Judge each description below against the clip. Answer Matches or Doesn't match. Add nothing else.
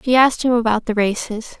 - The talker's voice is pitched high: Matches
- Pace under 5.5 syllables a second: Doesn't match